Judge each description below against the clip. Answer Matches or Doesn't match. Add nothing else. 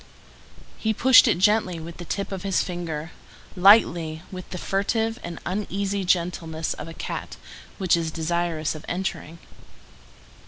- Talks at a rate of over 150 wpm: Doesn't match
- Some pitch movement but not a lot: Matches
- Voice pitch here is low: Doesn't match